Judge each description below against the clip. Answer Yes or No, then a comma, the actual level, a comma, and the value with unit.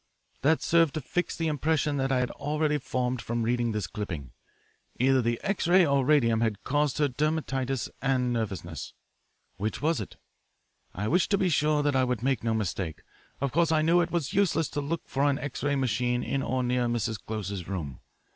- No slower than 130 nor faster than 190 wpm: No, average, 200 wpm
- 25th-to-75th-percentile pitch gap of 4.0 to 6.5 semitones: Yes, average, 4.7 semitones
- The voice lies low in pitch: Yes, low, 130 Hz